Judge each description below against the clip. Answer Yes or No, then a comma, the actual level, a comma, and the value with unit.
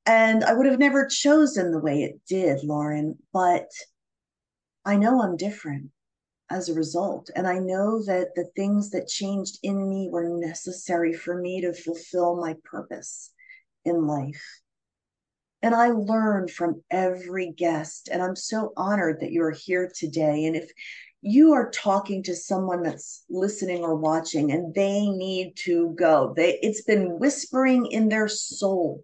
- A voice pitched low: No, medium, 180 Hz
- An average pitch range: Yes, average, 3.8 semitones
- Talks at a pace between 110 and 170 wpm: Yes, average, 160 wpm